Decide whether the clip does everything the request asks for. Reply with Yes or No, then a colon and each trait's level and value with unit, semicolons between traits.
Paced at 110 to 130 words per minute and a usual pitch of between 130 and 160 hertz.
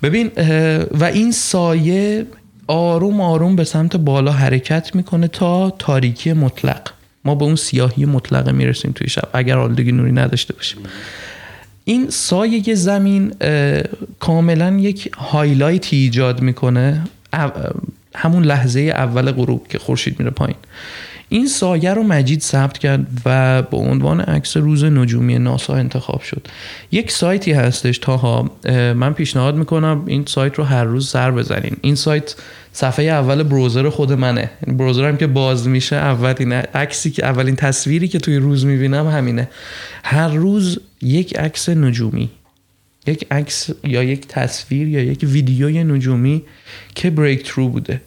No: average, 140 wpm; medium, 140 Hz